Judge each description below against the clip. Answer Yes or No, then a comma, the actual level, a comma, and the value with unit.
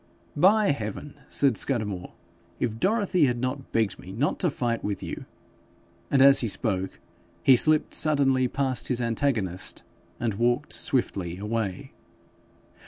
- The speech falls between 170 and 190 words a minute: No, average, 140 wpm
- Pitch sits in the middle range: No, low, 120 Hz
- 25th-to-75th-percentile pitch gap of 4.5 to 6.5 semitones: Yes, average, 5.1 semitones